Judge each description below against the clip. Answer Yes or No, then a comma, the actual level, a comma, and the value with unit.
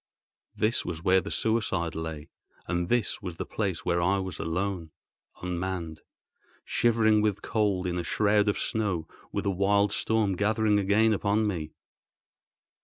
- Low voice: Yes, low, 100 Hz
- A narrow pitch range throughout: No, average, 3.5 semitones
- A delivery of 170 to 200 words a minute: No, average, 145 wpm